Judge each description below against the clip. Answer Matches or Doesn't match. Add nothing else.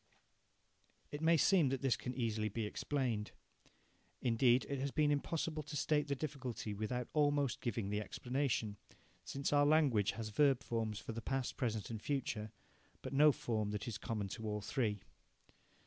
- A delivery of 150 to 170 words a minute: Matches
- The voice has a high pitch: Doesn't match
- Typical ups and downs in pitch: Matches